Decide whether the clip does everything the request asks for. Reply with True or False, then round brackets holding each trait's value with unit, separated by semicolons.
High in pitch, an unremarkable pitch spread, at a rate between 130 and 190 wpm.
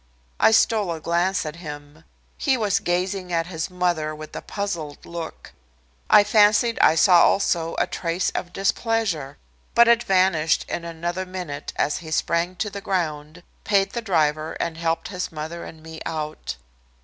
False (170 Hz; 3.5 semitones; 165 wpm)